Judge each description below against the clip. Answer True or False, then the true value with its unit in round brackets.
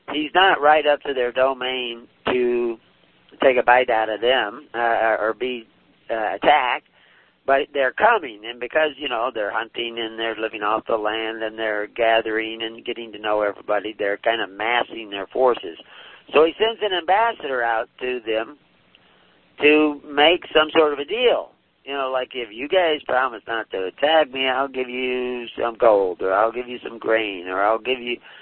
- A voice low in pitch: True (125 Hz)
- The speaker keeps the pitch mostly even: False (4.6 semitones)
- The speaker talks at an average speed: True (190 wpm)